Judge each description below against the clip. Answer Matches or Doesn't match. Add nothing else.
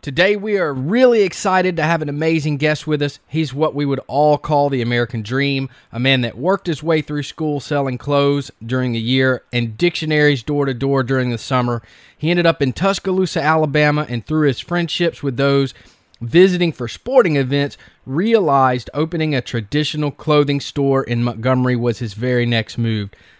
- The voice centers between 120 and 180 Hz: Matches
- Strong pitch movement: Doesn't match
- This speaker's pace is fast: Doesn't match